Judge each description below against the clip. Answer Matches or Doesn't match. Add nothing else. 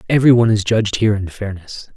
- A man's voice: Matches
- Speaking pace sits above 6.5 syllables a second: Matches